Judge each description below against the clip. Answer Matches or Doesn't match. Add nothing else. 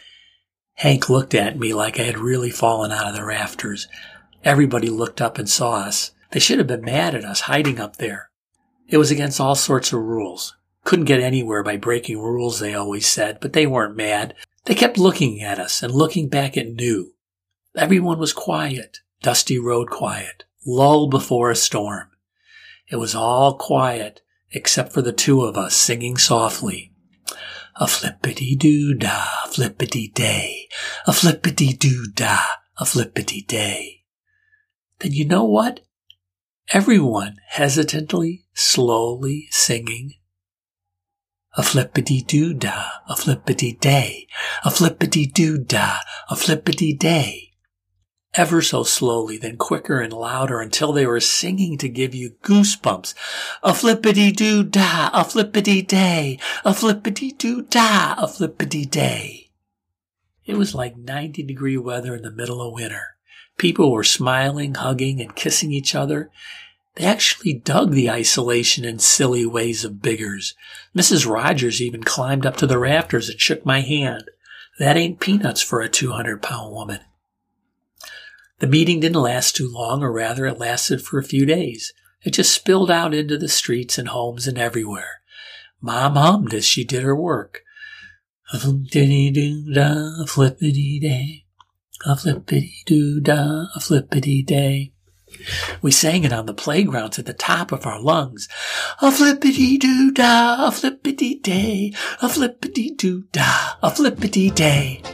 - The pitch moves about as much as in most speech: Doesn't match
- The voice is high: Doesn't match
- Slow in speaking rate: Doesn't match